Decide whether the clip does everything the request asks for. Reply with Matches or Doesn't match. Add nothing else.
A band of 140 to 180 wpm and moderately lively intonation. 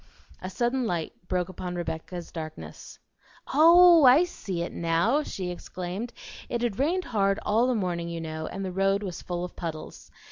Doesn't match